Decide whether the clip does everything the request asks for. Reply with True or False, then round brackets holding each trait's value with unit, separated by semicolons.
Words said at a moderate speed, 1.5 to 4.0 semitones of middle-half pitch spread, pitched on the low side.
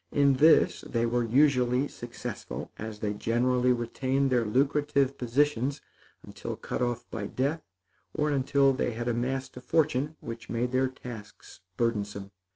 True (145 wpm; 2.9 semitones; 125 Hz)